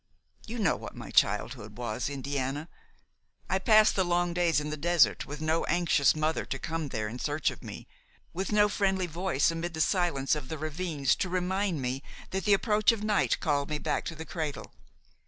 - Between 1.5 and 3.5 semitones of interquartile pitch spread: No, average, 4.5 semitones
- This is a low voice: No, medium, 160 Hz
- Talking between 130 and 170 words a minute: No, average, 195 wpm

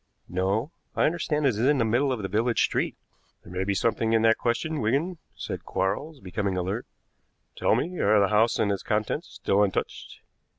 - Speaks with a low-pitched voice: Yes, low, 110 Hz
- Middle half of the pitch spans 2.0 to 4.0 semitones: No, wide, 5.5 semitones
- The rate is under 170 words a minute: No, average, 195 wpm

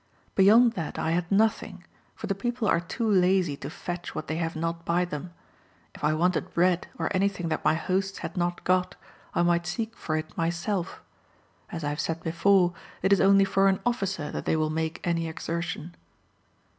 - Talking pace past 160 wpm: Yes, average, 195 wpm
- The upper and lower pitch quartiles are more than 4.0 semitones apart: No, average, 2.8 semitones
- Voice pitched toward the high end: No, medium, 175 Hz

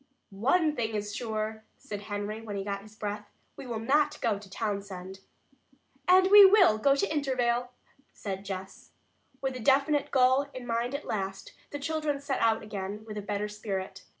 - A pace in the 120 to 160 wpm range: No, average, 175 wpm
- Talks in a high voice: Yes, high, 220 Hz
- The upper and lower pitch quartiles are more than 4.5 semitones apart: Yes, average, 5.2 semitones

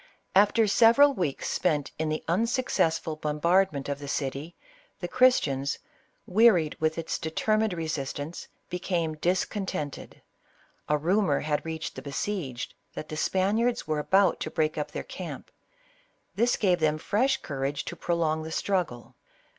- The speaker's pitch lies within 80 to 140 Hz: No, medium, 165 Hz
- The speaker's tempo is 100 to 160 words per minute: Yes, average, 140 wpm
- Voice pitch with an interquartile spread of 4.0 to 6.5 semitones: Yes, average, 4.8 semitones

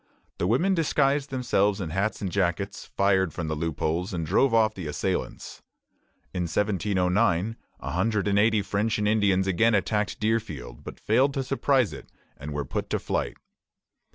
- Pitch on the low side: Yes, low, 100 Hz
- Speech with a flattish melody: No, average, 3.9 semitones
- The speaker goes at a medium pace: Yes, average, 165 wpm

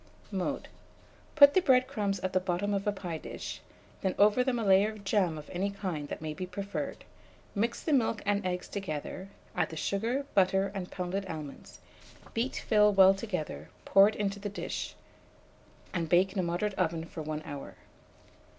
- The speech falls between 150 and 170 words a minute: No, average, 185 wpm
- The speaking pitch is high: Yes, high, 195 Hz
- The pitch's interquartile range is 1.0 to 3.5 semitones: Yes, average, 2.8 semitones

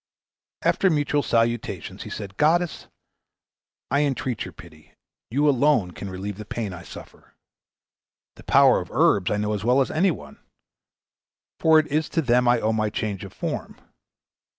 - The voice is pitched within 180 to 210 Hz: No, low, 120 Hz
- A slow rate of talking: No, average, 165 wpm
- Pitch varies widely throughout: Yes, wide, 6.1 semitones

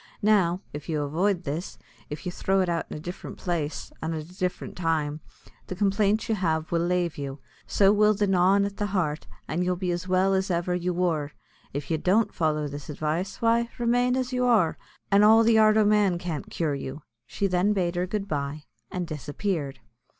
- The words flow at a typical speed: No, fast, 210 wpm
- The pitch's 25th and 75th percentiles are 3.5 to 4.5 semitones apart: Yes, average, 4.2 semitones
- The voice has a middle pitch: Yes, medium, 180 Hz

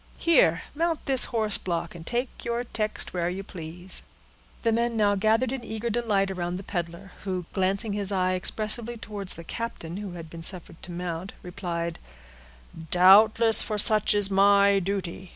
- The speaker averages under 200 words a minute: Yes, average, 165 wpm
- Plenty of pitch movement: No, average, 3.7 semitones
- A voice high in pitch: Yes, high, 195 Hz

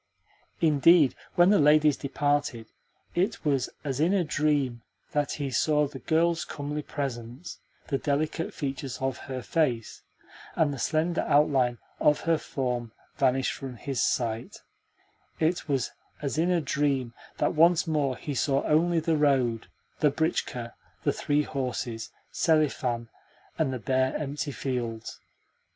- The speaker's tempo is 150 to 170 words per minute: No, average, 140 wpm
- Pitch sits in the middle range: Yes, medium, 145 Hz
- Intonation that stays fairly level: No, average, 3.2 semitones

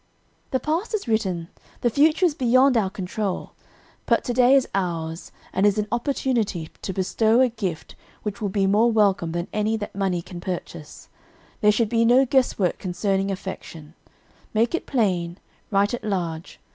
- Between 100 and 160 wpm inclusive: No, average, 170 wpm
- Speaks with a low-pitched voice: No, high, 205 Hz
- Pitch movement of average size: Yes, average, 4.6 semitones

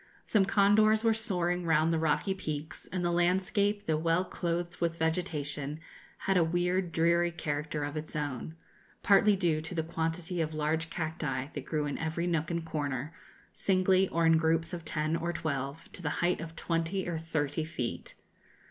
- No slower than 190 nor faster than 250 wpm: No, average, 175 wpm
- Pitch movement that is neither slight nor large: No, narrow, 2.3 semitones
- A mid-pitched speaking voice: Yes, medium, 165 Hz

